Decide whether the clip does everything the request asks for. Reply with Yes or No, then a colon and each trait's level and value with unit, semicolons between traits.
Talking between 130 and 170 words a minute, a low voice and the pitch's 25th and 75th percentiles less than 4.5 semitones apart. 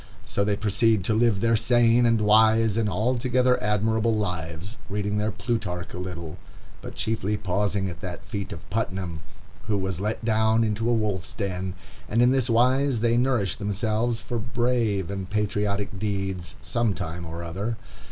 Yes: average, 165 wpm; low, 105 Hz; average, 3.0 semitones